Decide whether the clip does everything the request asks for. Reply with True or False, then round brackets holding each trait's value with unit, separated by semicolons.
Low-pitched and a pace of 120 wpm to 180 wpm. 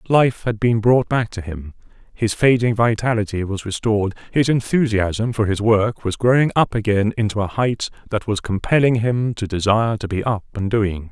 False (110 Hz; 190 wpm)